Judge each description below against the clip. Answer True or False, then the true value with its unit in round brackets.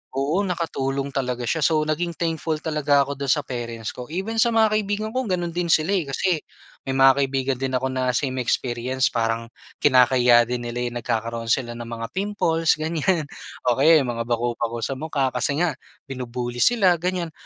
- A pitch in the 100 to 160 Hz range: True (140 Hz)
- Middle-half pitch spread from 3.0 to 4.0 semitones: False (5.5 semitones)